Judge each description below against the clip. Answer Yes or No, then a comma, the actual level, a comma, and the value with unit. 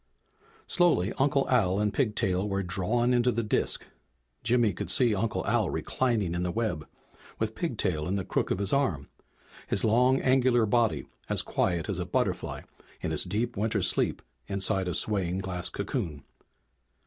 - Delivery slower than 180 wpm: Yes, average, 160 wpm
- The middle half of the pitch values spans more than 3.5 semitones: Yes, average, 4.6 semitones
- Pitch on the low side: Yes, low, 105 Hz